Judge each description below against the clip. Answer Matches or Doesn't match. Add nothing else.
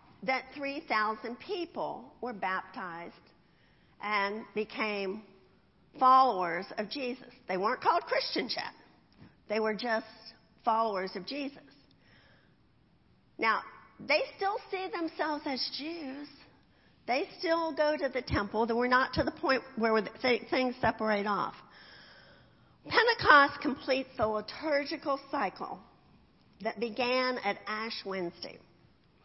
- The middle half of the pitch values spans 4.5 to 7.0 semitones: Matches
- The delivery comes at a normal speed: Doesn't match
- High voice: Matches